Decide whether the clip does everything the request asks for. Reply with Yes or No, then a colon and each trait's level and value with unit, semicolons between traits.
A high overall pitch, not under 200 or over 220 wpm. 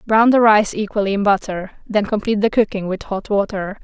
Yes: high, 205 Hz; fast, 205 wpm